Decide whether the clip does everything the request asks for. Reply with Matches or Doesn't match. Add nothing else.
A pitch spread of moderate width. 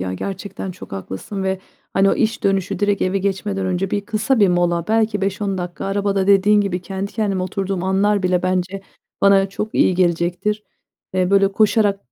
Doesn't match